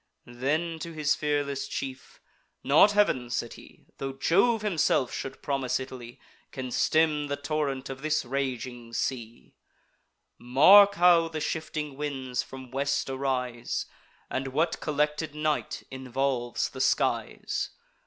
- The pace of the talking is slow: Yes, slow, 125 wpm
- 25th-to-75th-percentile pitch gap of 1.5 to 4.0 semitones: Yes, average, 3.0 semitones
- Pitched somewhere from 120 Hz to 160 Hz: Yes, medium, 140 Hz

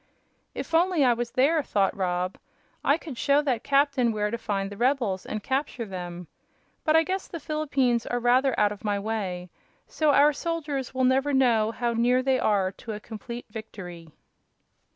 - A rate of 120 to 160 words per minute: No, average, 180 wpm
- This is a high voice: Yes, high, 240 Hz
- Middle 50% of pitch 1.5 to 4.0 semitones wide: No, average, 5.2 semitones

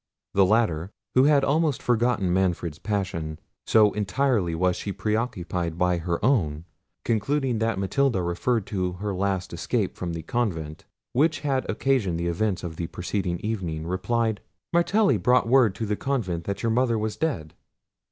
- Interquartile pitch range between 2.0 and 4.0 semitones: No, wide, 5.6 semitones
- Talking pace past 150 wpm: Yes, average, 160 wpm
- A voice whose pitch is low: Yes, low, 100 Hz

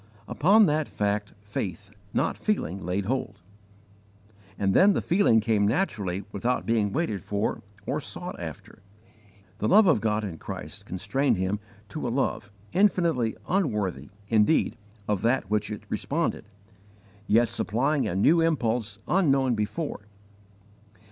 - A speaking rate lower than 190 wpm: Yes, slow, 135 wpm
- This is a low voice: Yes, low, 110 Hz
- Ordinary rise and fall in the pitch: No, wide, 6.5 semitones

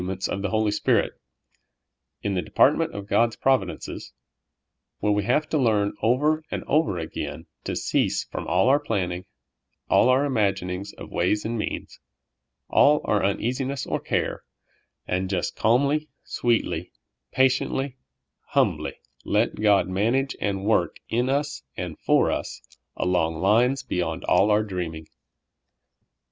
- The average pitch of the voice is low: Yes, low, 105 Hz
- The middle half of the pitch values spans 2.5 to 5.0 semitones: No, wide, 5.6 semitones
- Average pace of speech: Yes, average, 145 wpm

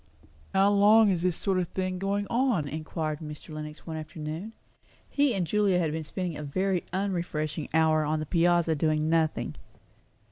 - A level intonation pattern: No, average, 3.8 semitones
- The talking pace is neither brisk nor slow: Yes, average, 170 wpm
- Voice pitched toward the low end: No, medium, 170 Hz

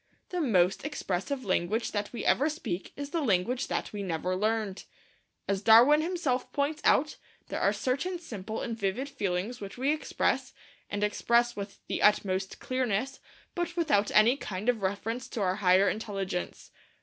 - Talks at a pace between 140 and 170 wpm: Yes, average, 160 wpm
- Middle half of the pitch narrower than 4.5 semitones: No, wide, 5.6 semitones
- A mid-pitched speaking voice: No, high, 225 Hz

